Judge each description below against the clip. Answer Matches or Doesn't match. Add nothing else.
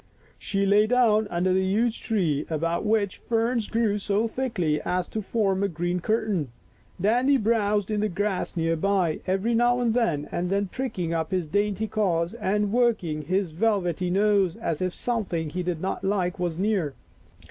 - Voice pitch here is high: Matches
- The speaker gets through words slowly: Doesn't match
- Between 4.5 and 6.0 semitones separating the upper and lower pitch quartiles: Doesn't match